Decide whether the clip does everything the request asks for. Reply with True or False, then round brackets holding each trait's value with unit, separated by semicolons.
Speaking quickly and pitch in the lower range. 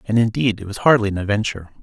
True (230 wpm; 105 Hz)